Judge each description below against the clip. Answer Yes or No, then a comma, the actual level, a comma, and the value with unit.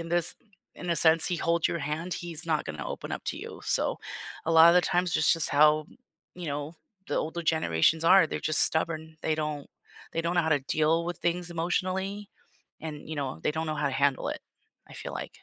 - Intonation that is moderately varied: No, narrow, 2.0 semitones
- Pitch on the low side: No, medium, 160 Hz